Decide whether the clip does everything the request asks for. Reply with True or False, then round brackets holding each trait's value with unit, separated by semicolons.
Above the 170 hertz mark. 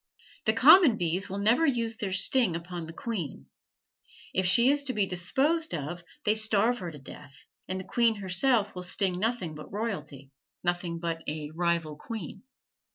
True (185 Hz)